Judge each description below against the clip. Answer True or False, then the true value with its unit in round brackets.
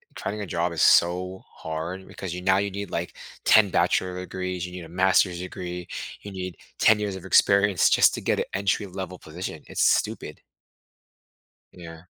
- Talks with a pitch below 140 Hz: True (90 Hz)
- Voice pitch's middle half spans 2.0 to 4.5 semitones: False (1.5 semitones)